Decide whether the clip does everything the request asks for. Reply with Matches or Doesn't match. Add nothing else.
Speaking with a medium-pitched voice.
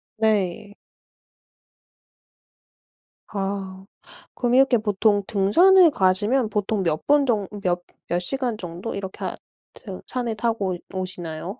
Doesn't match